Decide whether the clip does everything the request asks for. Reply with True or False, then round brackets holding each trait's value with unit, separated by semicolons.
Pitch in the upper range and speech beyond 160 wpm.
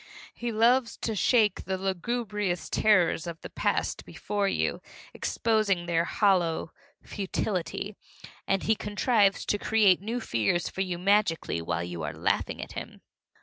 False (195 Hz; 145 wpm)